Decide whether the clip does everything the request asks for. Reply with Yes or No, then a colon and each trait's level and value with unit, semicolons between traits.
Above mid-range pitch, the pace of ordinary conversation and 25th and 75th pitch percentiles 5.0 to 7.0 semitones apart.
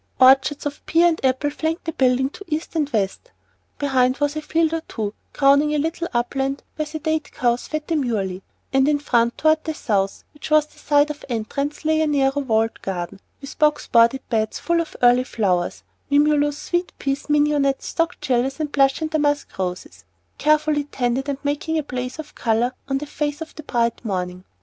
No: very high, 285 Hz; average, 190 wpm; average, 3.8 semitones